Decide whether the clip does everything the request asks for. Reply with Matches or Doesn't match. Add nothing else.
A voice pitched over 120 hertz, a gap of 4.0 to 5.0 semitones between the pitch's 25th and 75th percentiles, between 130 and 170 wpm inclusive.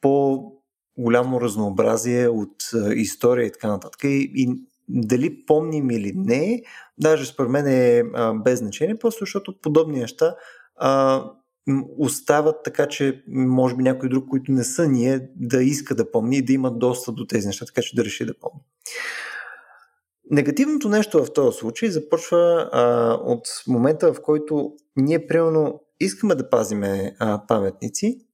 Matches